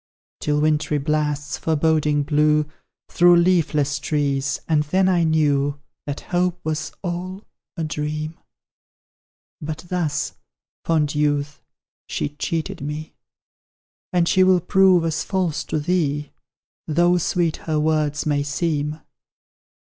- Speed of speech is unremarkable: No, slow, 115 wpm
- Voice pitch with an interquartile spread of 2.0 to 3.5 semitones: Yes, narrow, 2.6 semitones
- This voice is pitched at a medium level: Yes, medium, 155 Hz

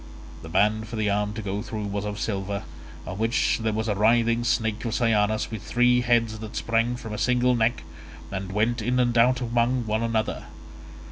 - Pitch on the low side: Yes, low, 110 Hz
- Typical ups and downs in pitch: No, narrow, 2.1 semitones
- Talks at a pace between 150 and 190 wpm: No, average, 200 wpm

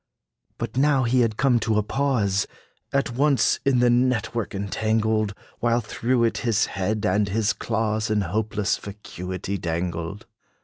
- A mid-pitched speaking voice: No, low, 110 Hz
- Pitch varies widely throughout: No, average, 3.2 semitones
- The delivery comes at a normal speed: Yes, average, 150 wpm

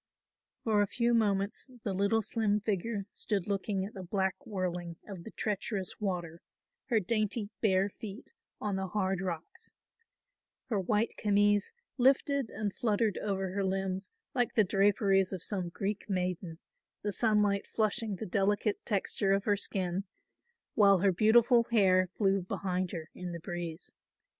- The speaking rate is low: No, average, 150 wpm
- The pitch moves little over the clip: Yes, narrow, 2.2 semitones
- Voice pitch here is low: No, high, 200 Hz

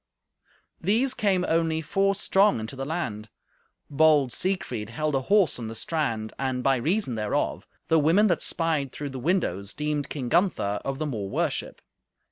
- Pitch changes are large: Yes, wide, 6.3 semitones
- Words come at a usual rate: Yes, average, 165 wpm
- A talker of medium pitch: Yes, medium, 150 Hz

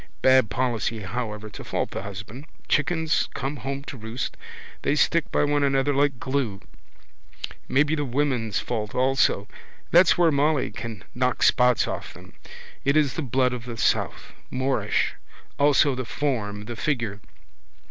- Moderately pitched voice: No, low, 130 Hz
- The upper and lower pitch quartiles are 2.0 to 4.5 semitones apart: Yes, average, 4.1 semitones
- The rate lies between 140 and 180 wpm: Yes, average, 145 wpm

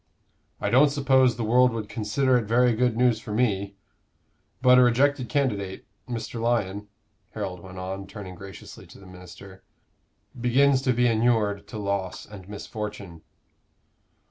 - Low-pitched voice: Yes, low, 110 Hz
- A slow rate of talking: No, average, 145 wpm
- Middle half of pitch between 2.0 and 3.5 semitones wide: No, average, 3.9 semitones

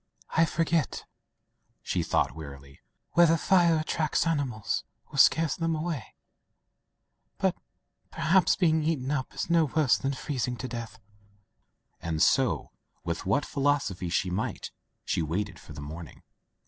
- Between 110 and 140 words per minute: Yes, slow, 135 wpm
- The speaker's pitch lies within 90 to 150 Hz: Yes, low, 135 Hz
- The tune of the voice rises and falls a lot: Yes, wide, 9.0 semitones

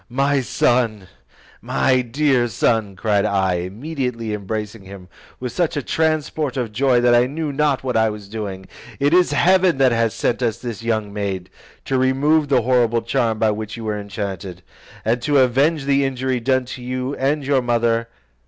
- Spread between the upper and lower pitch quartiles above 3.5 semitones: Yes, average, 4.0 semitones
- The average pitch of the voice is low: Yes, low, 120 Hz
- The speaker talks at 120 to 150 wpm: No, average, 180 wpm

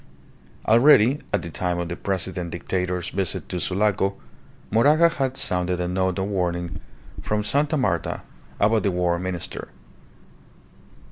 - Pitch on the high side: No, very low, 95 Hz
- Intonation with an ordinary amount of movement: Yes, average, 3.4 semitones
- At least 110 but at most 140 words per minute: Yes, slow, 135 wpm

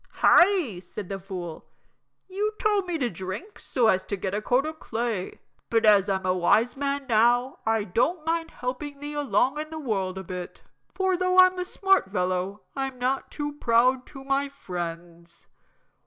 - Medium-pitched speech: No, high, 245 Hz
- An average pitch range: No, wide, 7.8 semitones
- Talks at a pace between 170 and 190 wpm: Yes, average, 180 wpm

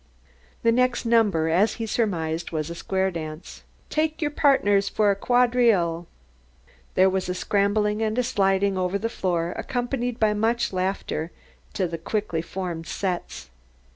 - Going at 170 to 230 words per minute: No, average, 150 wpm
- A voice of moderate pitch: No, high, 200 Hz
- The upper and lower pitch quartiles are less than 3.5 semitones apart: No, average, 4.7 semitones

